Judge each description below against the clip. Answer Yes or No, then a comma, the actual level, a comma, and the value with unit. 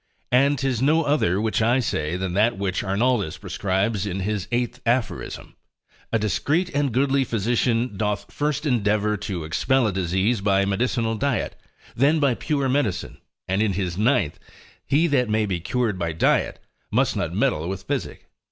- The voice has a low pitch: Yes, low, 110 Hz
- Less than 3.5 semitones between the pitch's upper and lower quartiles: No, average, 5.0 semitones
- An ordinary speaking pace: Yes, average, 165 wpm